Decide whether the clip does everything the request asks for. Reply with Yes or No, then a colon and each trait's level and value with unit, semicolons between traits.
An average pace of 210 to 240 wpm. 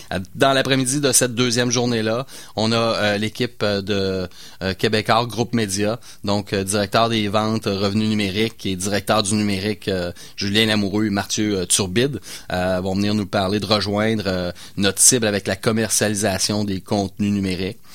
No: average, 165 wpm